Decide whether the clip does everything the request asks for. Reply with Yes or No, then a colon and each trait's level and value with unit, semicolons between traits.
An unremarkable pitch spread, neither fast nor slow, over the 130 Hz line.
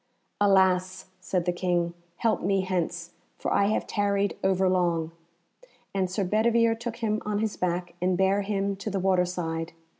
No: narrow, 2.2 semitones; average, 160 wpm; high, 190 Hz